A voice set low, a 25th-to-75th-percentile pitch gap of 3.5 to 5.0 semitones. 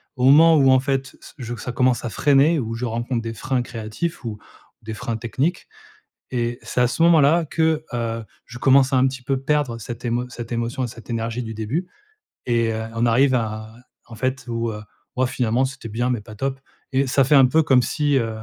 No: low, 125 Hz; average, 2.8 semitones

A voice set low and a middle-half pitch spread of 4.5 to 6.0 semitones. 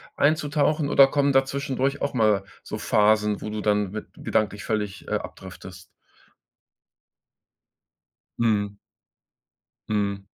Yes: low, 110 Hz; average, 5.1 semitones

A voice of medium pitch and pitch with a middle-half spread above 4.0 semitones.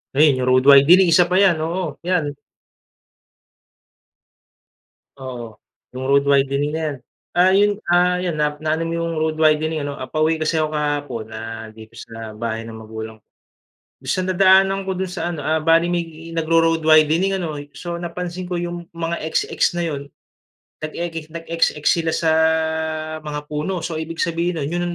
No: medium, 160 Hz; average, 3.3 semitones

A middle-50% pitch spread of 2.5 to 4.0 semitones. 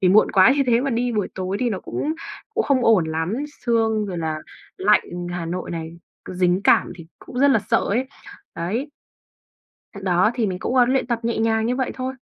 No: average, 5.2 semitones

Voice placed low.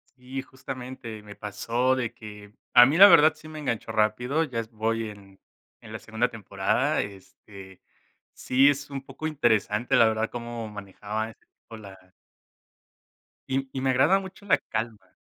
Yes: low, 115 Hz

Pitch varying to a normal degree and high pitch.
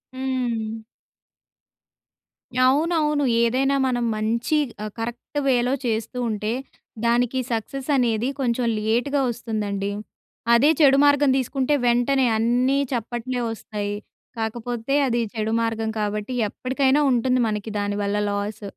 Yes: average, 3.0 semitones; high, 240 Hz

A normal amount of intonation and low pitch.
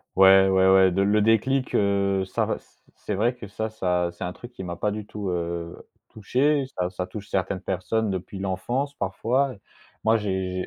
Yes: average, 3.0 semitones; low, 100 Hz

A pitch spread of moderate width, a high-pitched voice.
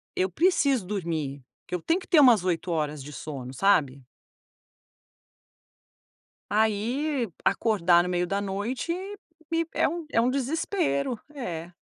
No: wide, 8.3 semitones; high, 200 Hz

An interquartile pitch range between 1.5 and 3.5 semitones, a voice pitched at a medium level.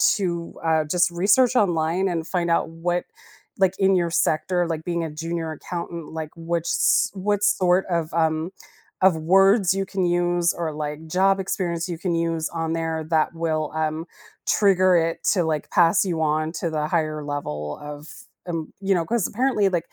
Yes: narrow, 2.6 semitones; medium, 170 Hz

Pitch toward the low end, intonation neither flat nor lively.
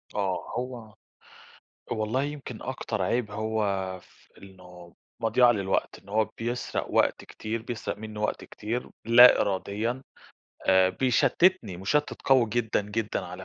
Yes: low, 110 Hz; average, 3.5 semitones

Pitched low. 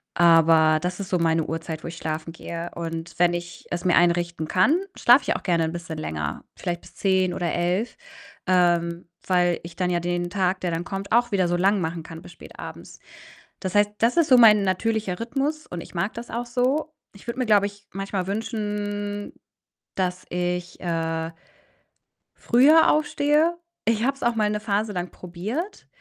No: medium, 185 Hz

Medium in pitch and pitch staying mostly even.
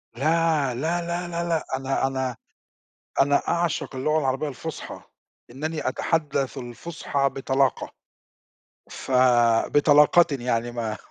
No: medium, 145 Hz; average, 3.7 semitones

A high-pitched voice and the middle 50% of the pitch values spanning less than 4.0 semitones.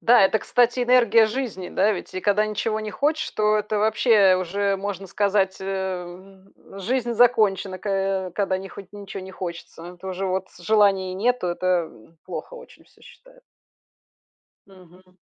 Yes: high, 195 Hz; narrow, 2.6 semitones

